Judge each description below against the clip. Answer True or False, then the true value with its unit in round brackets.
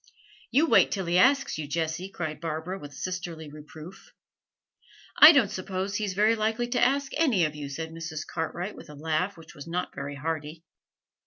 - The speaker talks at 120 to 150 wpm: False (180 wpm)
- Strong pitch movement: False (4.5 semitones)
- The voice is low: False (170 Hz)